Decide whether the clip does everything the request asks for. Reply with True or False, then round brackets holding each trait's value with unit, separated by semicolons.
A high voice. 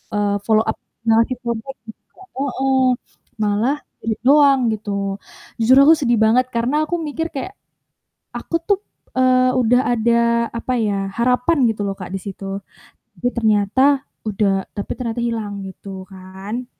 True (235 Hz)